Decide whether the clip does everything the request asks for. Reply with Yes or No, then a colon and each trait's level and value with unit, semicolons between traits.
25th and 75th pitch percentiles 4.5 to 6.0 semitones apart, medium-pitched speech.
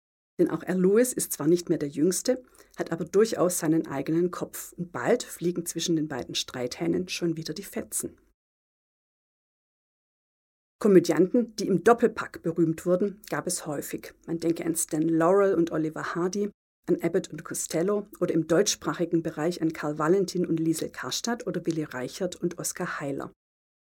No: narrow, 2.5 semitones; medium, 170 Hz